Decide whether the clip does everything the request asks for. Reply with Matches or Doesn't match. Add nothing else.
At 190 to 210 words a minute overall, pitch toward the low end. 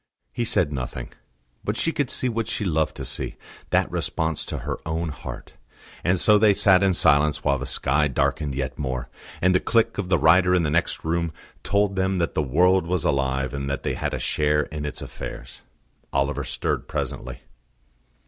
Matches